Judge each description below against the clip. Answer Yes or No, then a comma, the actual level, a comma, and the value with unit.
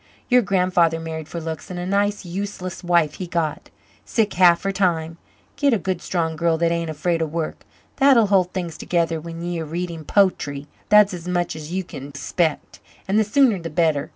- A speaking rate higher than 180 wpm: Yes, average, 195 wpm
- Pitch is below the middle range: No, medium, 175 Hz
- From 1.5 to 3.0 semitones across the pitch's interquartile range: Yes, average, 2.7 semitones